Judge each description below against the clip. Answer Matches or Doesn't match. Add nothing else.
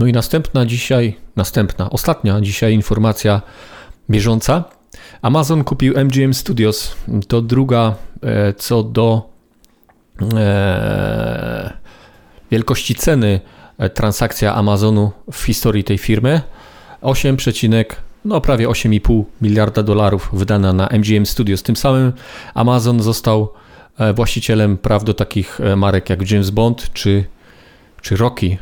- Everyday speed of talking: Doesn't match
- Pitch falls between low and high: Doesn't match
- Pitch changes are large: Doesn't match